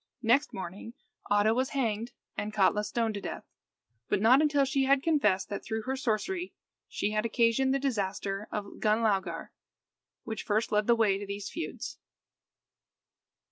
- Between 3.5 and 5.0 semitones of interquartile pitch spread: Yes, average, 4.3 semitones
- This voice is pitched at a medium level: No, high, 220 Hz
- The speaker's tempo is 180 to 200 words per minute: No, average, 155 wpm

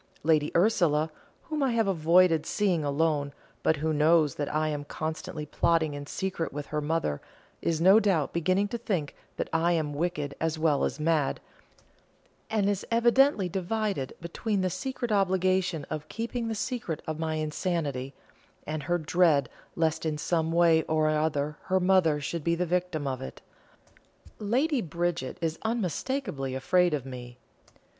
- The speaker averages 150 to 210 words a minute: Yes, average, 160 wpm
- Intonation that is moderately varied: Yes, average, 3.7 semitones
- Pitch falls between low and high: Yes, medium, 165 Hz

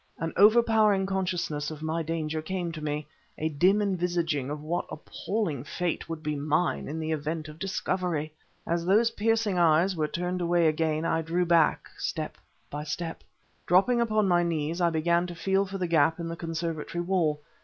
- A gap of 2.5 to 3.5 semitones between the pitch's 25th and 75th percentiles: Yes, average, 2.8 semitones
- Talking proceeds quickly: No, average, 180 wpm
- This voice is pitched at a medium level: Yes, medium, 170 Hz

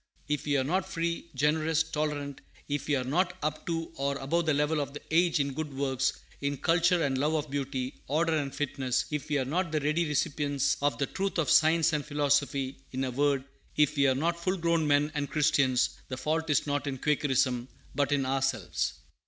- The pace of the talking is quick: Yes, fast, 210 wpm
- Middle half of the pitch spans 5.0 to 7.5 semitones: No, narrow, 2.5 semitones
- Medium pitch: Yes, medium, 145 Hz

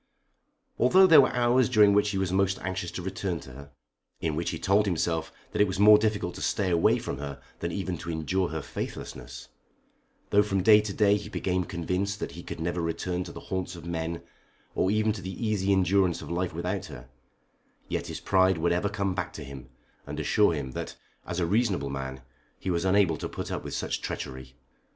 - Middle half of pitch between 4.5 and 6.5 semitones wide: No, average, 3.5 semitones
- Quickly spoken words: Yes, fast, 215 wpm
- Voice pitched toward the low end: Yes, very low, 95 Hz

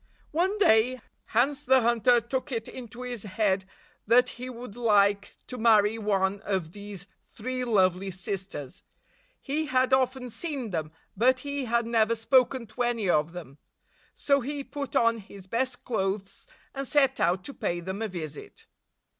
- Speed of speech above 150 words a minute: Yes, average, 160 wpm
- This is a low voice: No, high, 230 Hz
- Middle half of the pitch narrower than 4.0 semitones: No, average, 4.5 semitones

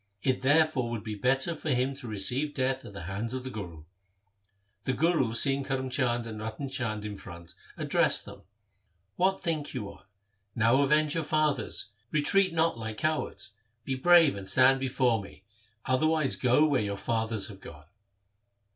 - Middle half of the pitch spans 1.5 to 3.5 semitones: No, average, 5.2 semitones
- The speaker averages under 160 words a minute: No, average, 175 wpm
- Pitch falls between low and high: No, low, 130 Hz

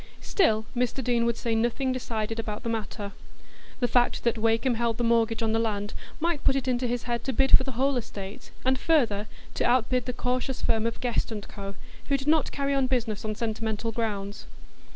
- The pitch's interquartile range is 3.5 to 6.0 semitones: No, narrow, 2.5 semitones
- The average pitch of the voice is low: No, high, 235 Hz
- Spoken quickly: Yes, fast, 210 wpm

